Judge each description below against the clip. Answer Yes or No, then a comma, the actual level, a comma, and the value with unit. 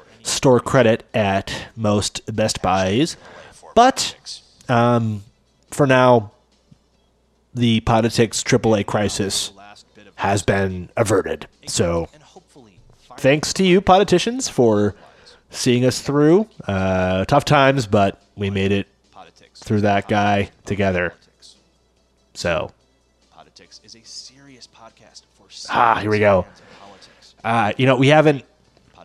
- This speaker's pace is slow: Yes, slow, 110 wpm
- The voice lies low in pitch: Yes, low, 110 Hz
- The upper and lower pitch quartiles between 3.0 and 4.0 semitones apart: No, average, 4.4 semitones